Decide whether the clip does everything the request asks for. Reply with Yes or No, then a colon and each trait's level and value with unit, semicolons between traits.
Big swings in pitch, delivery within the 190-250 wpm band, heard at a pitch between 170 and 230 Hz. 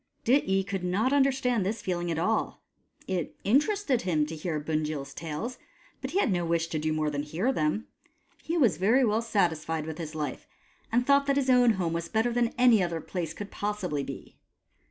Yes: wide, 7.1 semitones; average, 195 wpm; high, 190 Hz